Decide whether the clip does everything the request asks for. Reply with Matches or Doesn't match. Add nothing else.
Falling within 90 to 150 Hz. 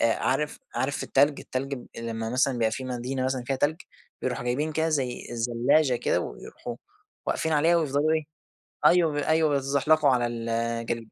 Matches